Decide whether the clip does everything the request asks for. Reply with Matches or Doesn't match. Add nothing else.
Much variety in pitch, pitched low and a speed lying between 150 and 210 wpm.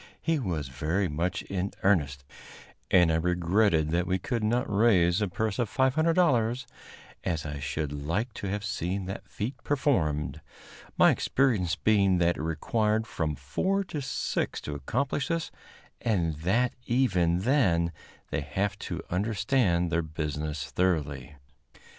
Doesn't match